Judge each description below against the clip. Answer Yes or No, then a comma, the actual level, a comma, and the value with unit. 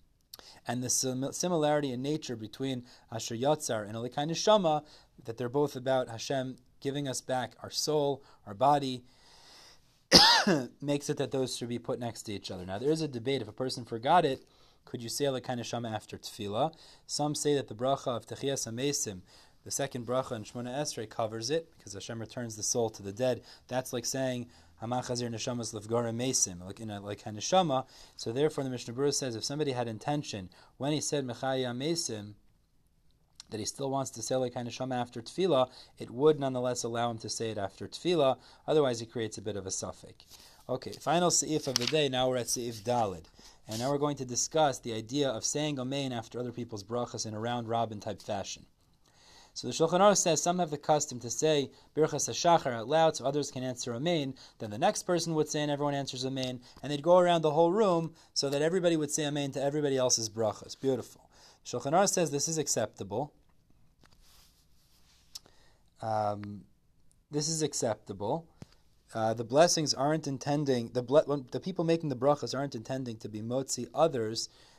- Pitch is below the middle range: Yes, low, 130 Hz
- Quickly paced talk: No, average, 190 wpm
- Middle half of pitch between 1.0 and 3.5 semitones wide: No, average, 3.9 semitones